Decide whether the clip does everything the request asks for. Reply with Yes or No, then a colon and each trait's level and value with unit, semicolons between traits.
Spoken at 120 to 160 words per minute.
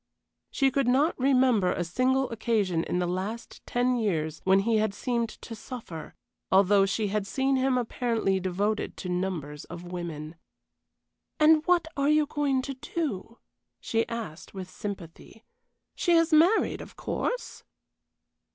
Yes: average, 145 wpm